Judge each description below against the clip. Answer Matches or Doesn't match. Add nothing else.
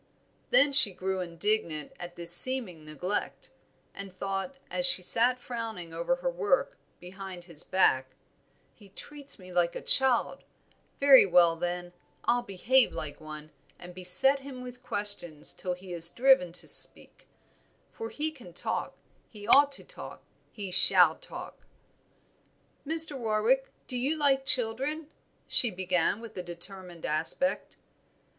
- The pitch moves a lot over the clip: Matches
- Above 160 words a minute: Doesn't match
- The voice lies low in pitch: Doesn't match